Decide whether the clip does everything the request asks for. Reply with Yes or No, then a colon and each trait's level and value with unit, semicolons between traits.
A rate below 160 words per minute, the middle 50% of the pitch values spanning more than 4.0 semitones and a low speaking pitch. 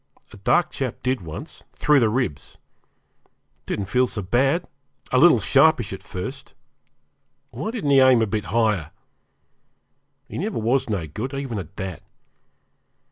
Yes: average, 150 wpm; wide, 5.4 semitones; low, 120 Hz